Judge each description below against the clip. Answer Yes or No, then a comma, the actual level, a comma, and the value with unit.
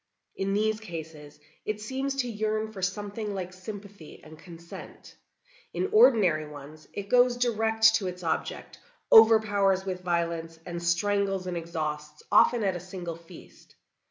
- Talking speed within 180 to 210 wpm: No, average, 145 wpm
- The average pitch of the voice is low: No, high, 195 Hz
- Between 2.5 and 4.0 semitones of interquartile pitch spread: No, average, 4.4 semitones